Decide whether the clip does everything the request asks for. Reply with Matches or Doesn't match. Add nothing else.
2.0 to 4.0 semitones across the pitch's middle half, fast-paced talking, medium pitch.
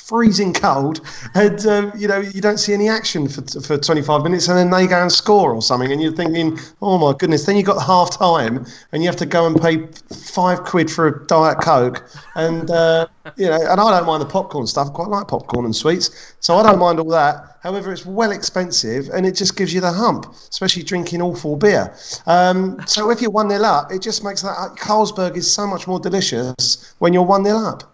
Matches